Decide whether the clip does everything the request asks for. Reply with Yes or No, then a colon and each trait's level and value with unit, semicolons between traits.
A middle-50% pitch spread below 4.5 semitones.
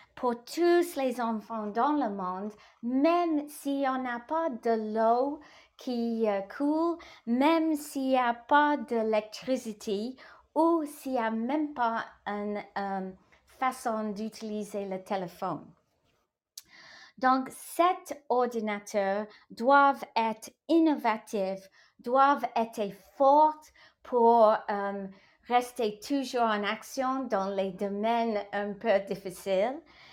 No: average, 5.1 semitones